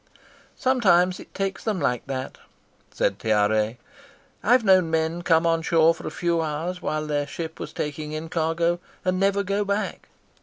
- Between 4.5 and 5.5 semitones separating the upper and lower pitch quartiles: No, average, 3.4 semitones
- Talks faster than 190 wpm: No, average, 165 wpm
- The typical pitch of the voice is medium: Yes, medium, 165 Hz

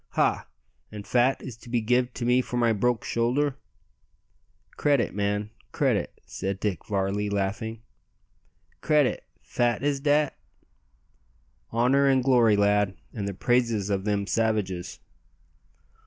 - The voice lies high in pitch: No, low, 115 Hz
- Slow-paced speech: Yes, slow, 125 wpm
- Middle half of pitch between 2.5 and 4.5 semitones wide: Yes, average, 3.6 semitones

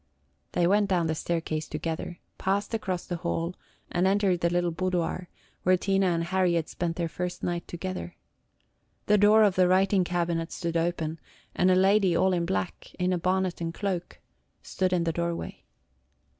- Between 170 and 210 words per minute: Yes, average, 175 wpm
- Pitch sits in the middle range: Yes, medium, 180 Hz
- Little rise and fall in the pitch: Yes, narrow, 1.9 semitones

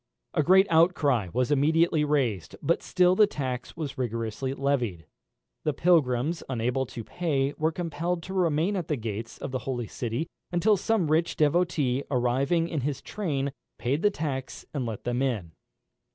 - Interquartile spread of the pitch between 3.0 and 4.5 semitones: No, average, 5.0 semitones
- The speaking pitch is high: No, medium, 140 Hz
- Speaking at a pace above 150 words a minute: Yes, average, 165 wpm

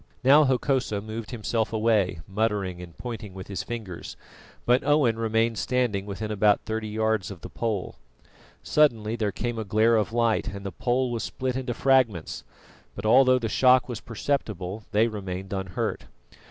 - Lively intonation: No, average, 3.2 semitones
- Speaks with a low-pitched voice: Yes, low, 110 Hz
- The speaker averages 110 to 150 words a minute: No, average, 165 wpm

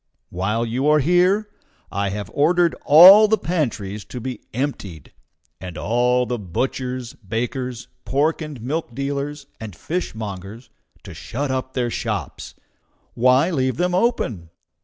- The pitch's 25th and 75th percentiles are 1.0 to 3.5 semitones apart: No, average, 5.3 semitones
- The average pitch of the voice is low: Yes, low, 130 Hz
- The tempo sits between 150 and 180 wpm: No, slow, 135 wpm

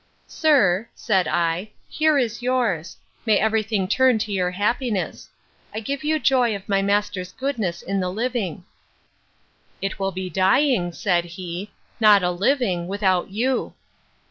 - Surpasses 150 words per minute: No, average, 145 wpm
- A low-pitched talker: No, high, 205 Hz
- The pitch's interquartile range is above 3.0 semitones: Yes, average, 4.8 semitones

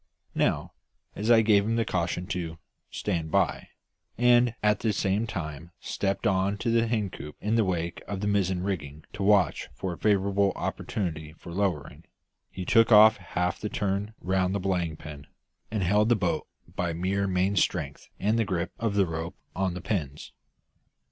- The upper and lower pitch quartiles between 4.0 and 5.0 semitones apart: No, average, 3.3 semitones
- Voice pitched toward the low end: Yes, very low, 95 Hz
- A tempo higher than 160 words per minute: Yes, average, 180 wpm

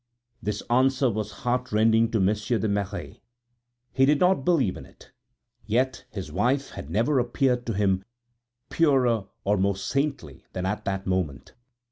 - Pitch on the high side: No, low, 110 Hz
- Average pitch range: Yes, average, 5.0 semitones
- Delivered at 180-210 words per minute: No, average, 150 wpm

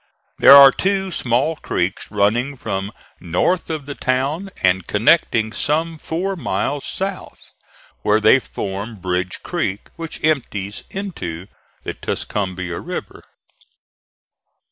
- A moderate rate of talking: No, slow, 115 wpm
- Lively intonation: Yes, wide, 8.6 semitones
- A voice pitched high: No, low, 125 Hz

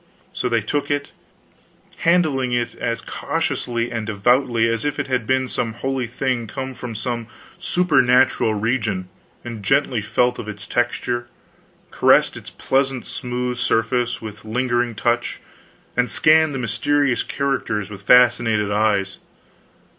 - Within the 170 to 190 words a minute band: No, slow, 135 wpm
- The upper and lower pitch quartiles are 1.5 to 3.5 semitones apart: Yes, average, 2.7 semitones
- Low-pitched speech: Yes, low, 120 Hz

